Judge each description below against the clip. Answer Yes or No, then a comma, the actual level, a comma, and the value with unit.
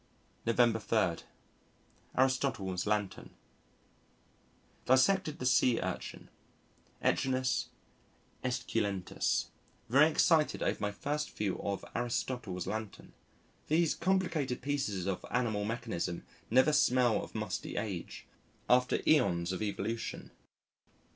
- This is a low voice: Yes, low, 120 Hz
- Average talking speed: No, slow, 95 wpm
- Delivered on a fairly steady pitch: No, average, 4.5 semitones